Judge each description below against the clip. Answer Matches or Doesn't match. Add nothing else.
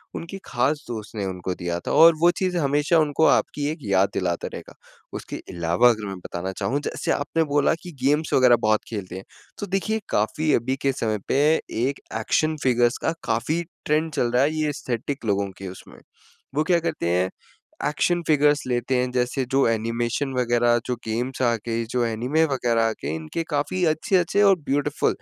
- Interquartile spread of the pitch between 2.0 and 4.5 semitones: Doesn't match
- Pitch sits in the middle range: Doesn't match